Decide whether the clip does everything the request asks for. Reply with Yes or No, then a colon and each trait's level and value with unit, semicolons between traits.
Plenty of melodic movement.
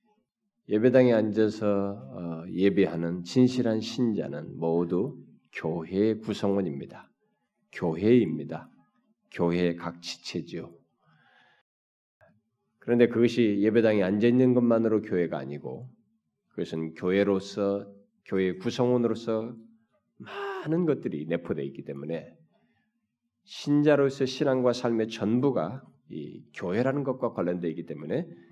Yes: wide, 6.5 semitones